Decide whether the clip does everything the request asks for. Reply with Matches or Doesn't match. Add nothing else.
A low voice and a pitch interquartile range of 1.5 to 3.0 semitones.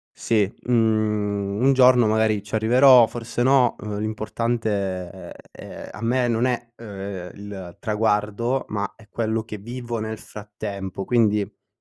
Matches